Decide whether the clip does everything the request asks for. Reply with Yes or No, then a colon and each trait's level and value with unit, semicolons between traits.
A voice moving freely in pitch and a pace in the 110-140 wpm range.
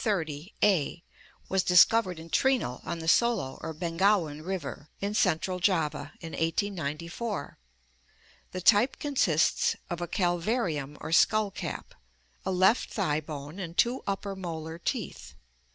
No: average, 4.0 semitones; slow, 135 wpm